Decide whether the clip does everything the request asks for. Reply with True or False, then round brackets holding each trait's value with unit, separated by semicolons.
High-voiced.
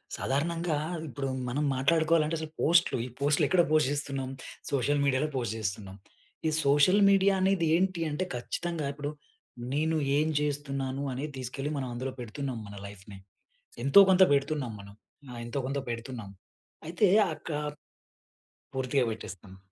False (140 Hz)